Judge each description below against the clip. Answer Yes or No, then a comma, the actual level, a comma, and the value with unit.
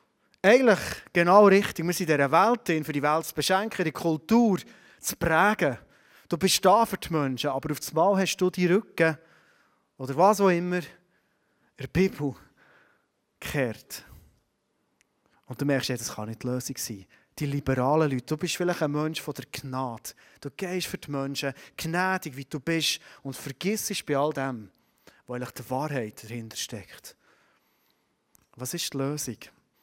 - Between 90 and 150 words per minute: No, average, 165 wpm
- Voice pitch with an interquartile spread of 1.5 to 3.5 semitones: No, average, 5.0 semitones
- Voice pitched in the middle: Yes, medium, 150 Hz